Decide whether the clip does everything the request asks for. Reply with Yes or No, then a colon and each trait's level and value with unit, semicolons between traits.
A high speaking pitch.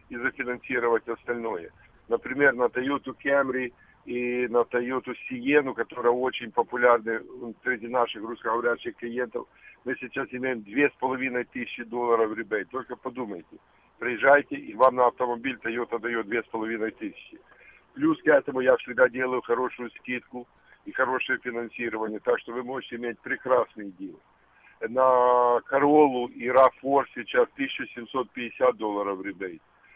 No: low, 125 Hz